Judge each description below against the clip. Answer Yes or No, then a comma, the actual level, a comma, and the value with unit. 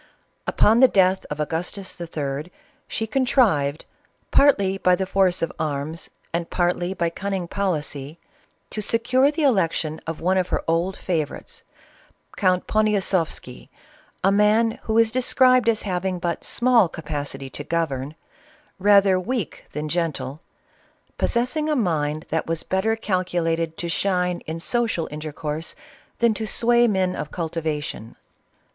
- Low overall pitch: No, medium, 180 Hz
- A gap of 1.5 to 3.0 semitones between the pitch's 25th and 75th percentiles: No, average, 4.9 semitones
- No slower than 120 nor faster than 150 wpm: Yes, average, 140 wpm